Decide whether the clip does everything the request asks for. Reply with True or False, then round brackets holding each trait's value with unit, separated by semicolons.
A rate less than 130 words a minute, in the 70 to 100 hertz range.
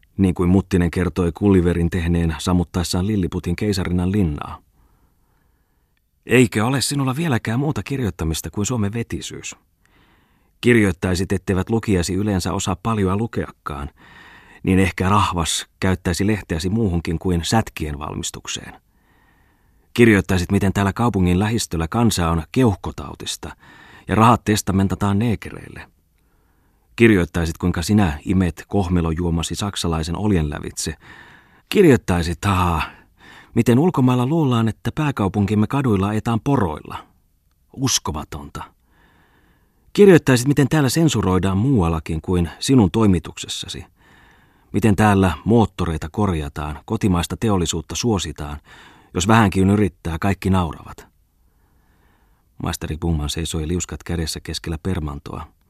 True (100 wpm; 95 Hz)